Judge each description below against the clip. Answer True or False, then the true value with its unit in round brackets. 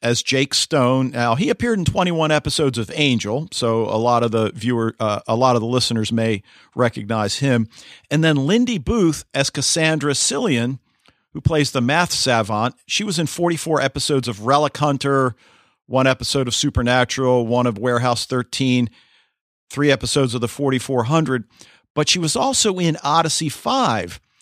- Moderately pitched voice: False (130 Hz)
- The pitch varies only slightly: False (4.0 semitones)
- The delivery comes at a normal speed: True (160 wpm)